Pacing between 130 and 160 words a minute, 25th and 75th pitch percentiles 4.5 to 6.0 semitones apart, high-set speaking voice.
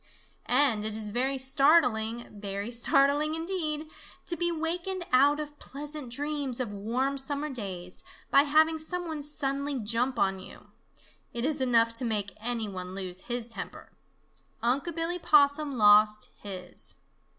Yes: average, 145 wpm; wide, 5.5 semitones; very high, 265 Hz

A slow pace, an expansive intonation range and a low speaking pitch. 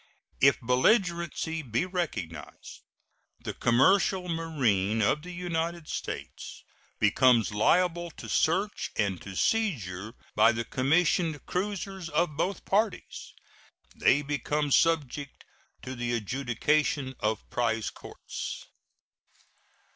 No: slow, 100 wpm; wide, 6.6 semitones; medium, 145 Hz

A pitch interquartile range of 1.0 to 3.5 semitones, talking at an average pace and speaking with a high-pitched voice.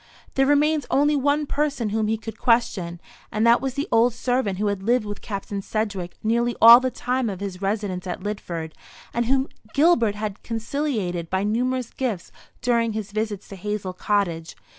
No: average, 4.1 semitones; average, 180 wpm; high, 220 Hz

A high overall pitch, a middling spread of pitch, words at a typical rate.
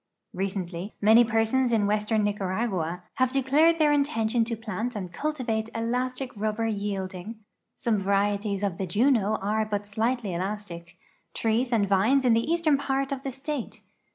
Yes: high, 220 Hz; average, 4.0 semitones; average, 155 wpm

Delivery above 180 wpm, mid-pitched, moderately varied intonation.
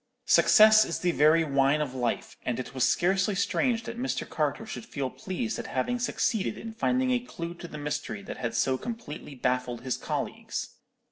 No: average, 190 wpm; medium, 170 Hz; wide, 8.5 semitones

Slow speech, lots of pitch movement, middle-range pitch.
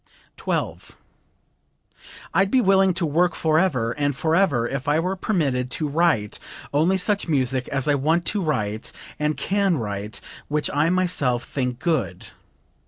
No: average, 145 wpm; wide, 5.8 semitones; medium, 150 Hz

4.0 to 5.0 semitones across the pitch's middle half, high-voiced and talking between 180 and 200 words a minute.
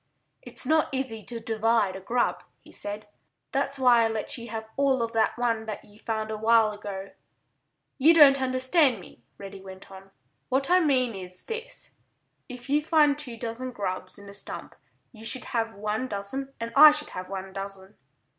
Yes: average, 4.4 semitones; high, 230 Hz; average, 185 wpm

